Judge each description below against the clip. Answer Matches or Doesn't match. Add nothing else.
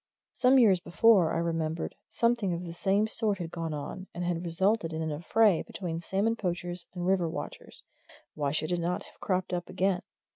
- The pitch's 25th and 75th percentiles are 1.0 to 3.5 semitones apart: Matches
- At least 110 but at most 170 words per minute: Doesn't match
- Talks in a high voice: Doesn't match